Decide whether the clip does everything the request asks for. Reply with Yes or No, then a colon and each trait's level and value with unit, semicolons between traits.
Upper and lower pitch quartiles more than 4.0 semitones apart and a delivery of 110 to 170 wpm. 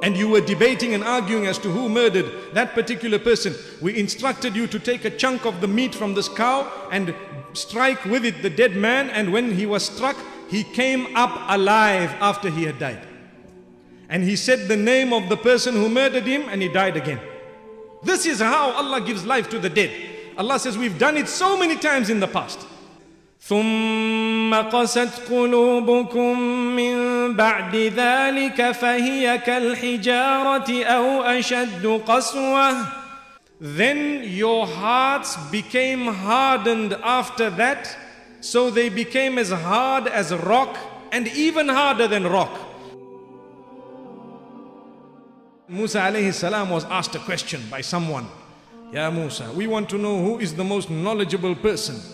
No: average, 3.7 semitones; average, 150 wpm